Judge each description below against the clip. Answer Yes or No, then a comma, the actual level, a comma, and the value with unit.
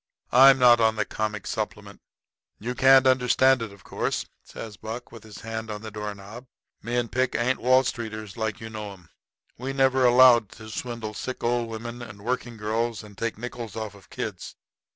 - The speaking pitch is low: Yes, low, 115 Hz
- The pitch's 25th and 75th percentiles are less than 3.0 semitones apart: Yes, narrow, 2.5 semitones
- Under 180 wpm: No, average, 195 wpm